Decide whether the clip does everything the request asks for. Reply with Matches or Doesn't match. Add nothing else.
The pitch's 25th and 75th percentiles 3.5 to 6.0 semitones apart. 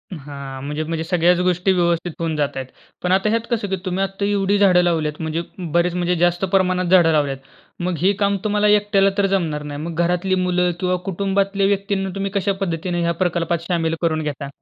Doesn't match